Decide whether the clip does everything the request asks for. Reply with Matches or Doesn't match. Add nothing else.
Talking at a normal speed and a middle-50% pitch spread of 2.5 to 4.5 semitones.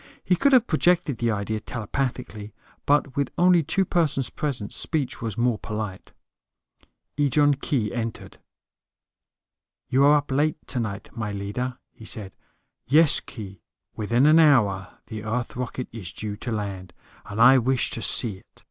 Doesn't match